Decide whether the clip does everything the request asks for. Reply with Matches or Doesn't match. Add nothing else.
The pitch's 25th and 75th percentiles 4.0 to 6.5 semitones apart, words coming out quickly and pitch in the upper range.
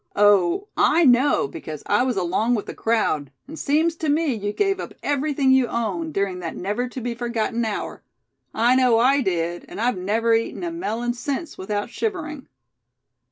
Doesn't match